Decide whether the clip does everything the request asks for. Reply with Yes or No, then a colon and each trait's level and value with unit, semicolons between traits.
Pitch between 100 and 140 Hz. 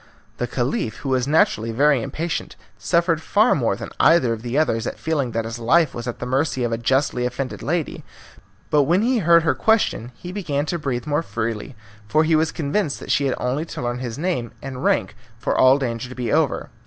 Yes: low, 135 Hz